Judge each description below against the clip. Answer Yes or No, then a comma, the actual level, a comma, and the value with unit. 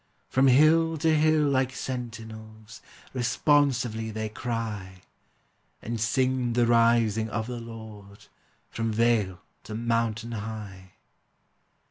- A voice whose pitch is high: No, low, 115 Hz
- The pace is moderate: No, slow, 105 wpm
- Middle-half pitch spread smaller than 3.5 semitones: Yes, narrow, 2.6 semitones